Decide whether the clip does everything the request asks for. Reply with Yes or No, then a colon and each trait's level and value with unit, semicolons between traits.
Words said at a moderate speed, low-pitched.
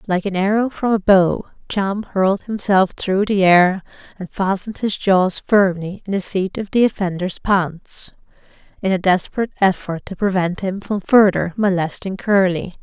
No: average, 165 wpm; high, 195 Hz